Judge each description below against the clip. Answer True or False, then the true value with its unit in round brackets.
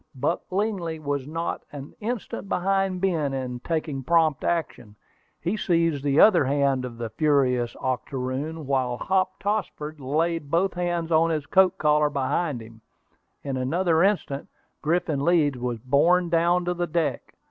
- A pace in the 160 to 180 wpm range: False (145 wpm)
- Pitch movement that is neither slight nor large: True (4.2 semitones)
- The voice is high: False (155 Hz)